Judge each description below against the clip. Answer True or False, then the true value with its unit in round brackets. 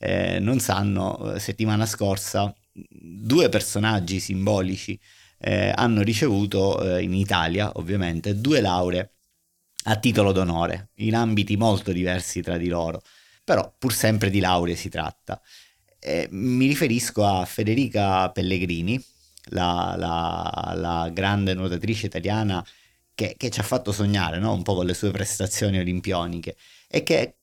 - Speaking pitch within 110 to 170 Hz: False (100 Hz)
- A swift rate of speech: False (135 wpm)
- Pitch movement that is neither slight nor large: True (3.0 semitones)